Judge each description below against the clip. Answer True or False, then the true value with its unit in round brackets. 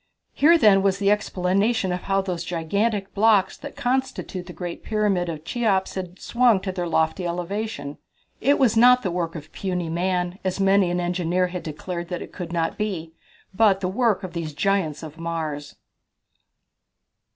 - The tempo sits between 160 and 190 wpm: True (175 wpm)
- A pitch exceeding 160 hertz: True (185 Hz)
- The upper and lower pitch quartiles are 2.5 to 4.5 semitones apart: True (3.3 semitones)